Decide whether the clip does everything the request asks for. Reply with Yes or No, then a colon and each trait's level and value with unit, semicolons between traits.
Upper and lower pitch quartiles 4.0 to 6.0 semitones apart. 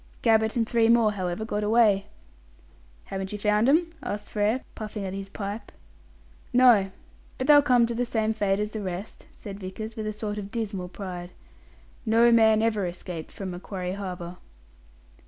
No: average, 2.7 semitones